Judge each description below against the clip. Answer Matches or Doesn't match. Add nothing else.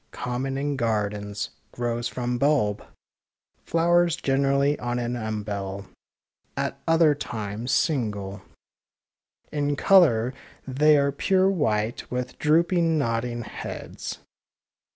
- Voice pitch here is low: Matches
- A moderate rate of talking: Doesn't match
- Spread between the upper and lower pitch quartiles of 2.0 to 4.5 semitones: Doesn't match